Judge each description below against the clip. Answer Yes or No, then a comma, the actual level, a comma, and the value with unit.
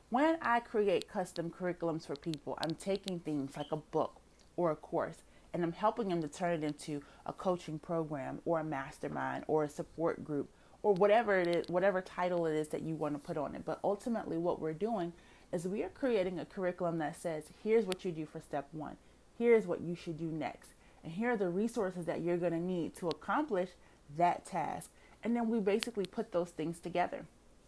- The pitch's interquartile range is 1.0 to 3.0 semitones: No, average, 3.6 semitones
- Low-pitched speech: No, medium, 170 Hz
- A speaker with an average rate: No, fast, 210 wpm